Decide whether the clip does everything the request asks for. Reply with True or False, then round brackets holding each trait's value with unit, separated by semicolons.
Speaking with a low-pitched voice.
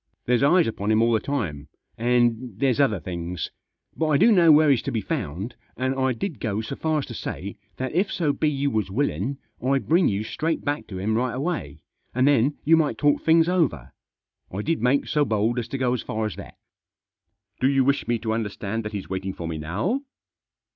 True (125 Hz)